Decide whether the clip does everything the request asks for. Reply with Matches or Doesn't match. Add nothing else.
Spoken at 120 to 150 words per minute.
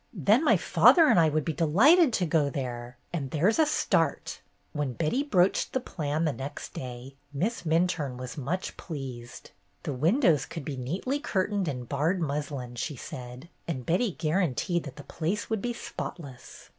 Doesn't match